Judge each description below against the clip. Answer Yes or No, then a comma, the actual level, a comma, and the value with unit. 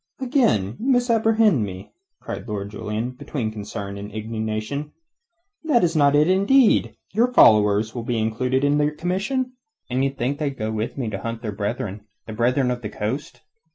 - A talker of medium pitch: No, low, 125 Hz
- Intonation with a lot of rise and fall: Yes, wide, 6.9 semitones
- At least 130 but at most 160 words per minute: No, average, 175 wpm